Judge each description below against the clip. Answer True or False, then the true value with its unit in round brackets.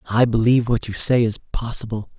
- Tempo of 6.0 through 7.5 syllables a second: True (6.2 syllables/s)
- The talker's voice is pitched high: False (115 Hz)